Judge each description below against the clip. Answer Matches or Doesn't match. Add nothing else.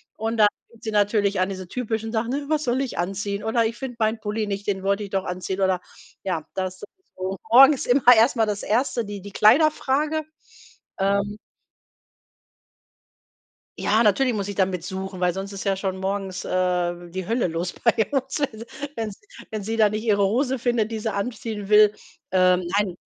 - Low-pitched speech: Doesn't match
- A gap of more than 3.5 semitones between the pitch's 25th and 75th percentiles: Doesn't match